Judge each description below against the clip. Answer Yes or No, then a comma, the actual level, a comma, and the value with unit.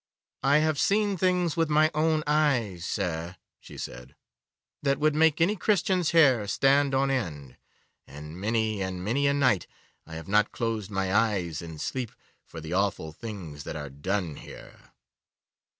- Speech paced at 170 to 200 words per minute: No, average, 160 wpm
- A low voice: Yes, low, 110 Hz